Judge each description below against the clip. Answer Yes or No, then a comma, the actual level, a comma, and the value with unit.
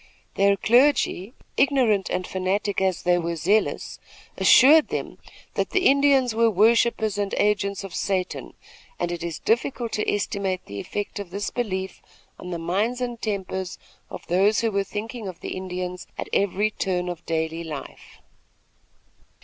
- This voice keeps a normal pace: Yes, average, 155 wpm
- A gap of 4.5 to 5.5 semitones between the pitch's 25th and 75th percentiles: No, average, 3.7 semitones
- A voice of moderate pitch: No, high, 200 Hz